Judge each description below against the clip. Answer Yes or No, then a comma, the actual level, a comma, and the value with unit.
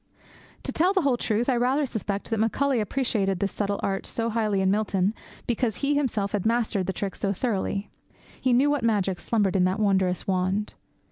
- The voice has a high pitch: Yes, high, 215 Hz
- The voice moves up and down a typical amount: Yes, average, 3.8 semitones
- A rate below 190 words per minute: No, average, 195 wpm